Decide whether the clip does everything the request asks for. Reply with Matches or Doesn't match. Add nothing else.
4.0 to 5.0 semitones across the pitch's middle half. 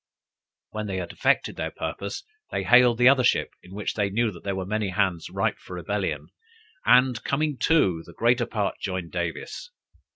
Matches